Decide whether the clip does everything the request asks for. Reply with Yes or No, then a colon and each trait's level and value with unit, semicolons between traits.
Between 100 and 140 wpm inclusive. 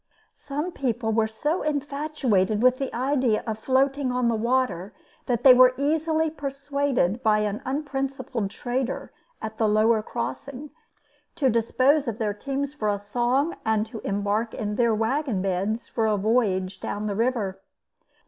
No: average, 155 wpm